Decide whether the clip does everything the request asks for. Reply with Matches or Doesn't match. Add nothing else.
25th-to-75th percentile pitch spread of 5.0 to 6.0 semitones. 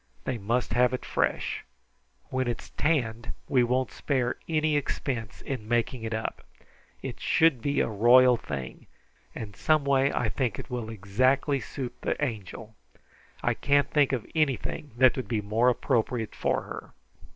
Doesn't match